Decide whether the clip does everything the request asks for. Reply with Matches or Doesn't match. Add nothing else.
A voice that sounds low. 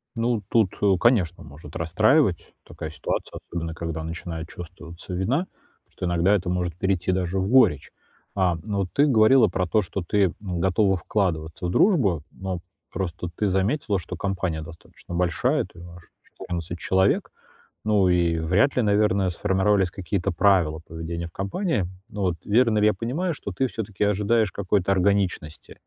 Matches